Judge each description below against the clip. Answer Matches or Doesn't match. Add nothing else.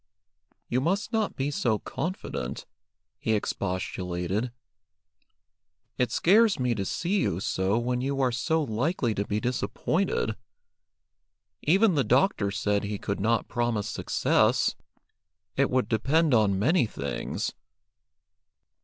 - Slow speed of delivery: Matches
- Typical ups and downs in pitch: Doesn't match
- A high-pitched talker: Doesn't match